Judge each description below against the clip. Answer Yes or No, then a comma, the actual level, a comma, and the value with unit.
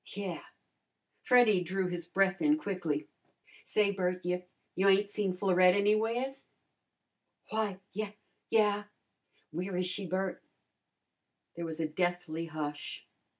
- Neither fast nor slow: No, slow, 120 wpm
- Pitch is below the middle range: No, high, 190 Hz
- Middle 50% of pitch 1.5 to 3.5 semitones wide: Yes, average, 2.7 semitones